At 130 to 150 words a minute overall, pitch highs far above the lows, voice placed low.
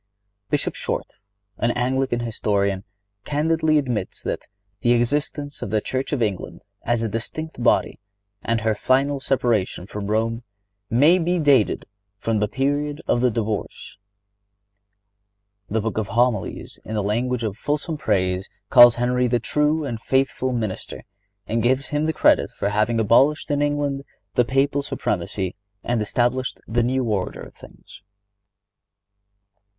No: average, 145 wpm; average, 4.4 semitones; low, 120 Hz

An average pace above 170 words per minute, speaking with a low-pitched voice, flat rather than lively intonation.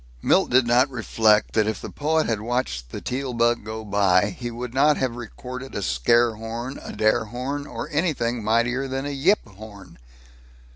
No: average, 185 wpm; low, 120 Hz; average, 3.2 semitones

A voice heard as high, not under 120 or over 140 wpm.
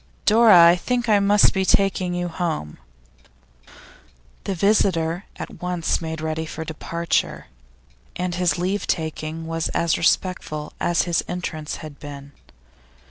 No: medium, 170 Hz; slow, 135 wpm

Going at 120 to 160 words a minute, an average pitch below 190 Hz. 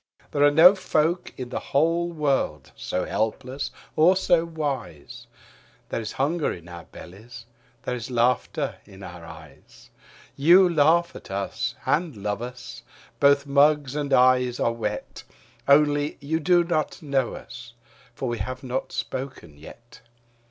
Yes: average, 145 wpm; low, 135 Hz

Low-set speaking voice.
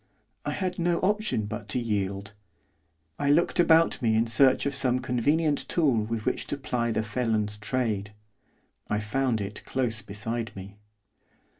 Yes: low, 115 Hz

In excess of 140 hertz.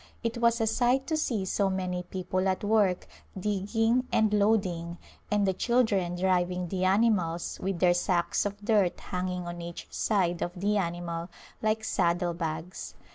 Yes: high, 190 Hz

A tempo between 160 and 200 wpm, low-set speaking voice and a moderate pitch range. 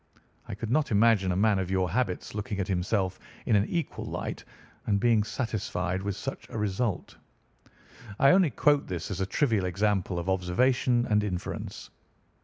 Yes: average, 170 wpm; low, 100 Hz; average, 3.7 semitones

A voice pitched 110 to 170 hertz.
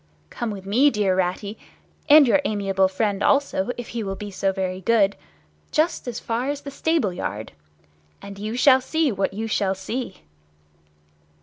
No: high, 210 Hz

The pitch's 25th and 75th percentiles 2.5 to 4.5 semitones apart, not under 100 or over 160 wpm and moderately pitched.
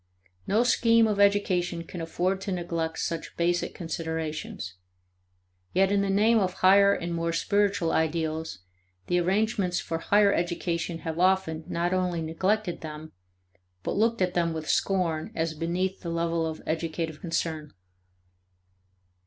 Yes: average, 2.9 semitones; average, 140 wpm; medium, 175 Hz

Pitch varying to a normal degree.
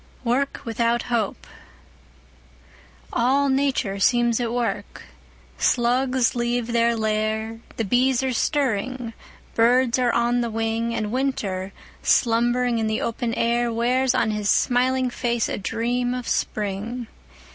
No: narrow, 1.8 semitones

